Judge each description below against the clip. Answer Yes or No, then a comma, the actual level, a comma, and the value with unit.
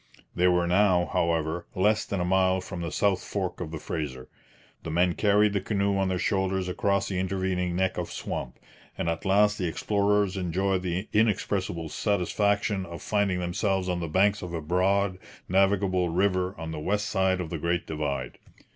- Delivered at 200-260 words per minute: No, average, 180 wpm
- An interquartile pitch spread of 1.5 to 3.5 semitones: Yes, narrow, 2.4 semitones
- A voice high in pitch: No, very low, 95 Hz